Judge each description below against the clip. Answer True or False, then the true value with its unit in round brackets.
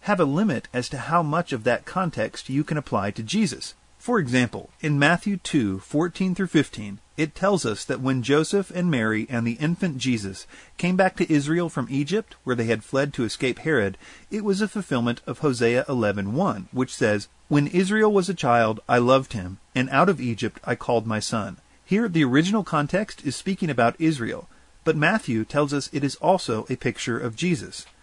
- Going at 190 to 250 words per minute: True (200 wpm)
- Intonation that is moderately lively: False (6.6 semitones)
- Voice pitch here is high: False (140 Hz)